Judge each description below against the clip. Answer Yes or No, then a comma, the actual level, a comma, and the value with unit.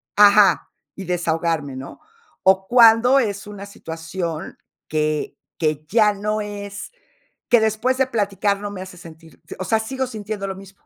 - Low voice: No, high, 200 Hz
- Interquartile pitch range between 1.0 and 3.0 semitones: No, average, 4.2 semitones